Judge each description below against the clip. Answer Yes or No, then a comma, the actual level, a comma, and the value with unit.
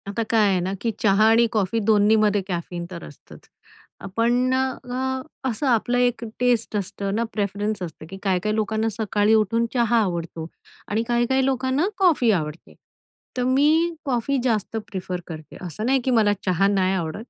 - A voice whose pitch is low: No, high, 220 Hz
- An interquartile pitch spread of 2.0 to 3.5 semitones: No, average, 4.2 semitones